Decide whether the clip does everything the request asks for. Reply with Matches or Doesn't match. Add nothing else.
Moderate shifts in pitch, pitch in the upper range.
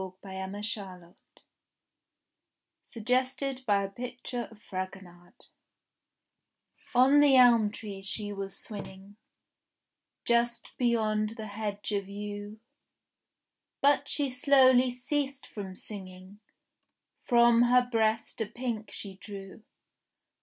Matches